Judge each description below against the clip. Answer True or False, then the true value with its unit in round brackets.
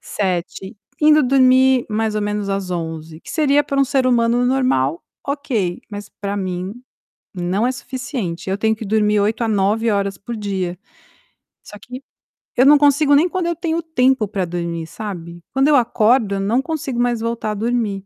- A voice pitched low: False (220 Hz)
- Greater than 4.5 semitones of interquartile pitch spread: True (5.1 semitones)